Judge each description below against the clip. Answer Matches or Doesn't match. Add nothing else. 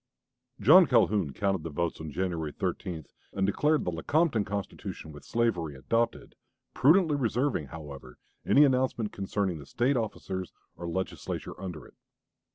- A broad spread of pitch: Matches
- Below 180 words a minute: Matches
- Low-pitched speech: Matches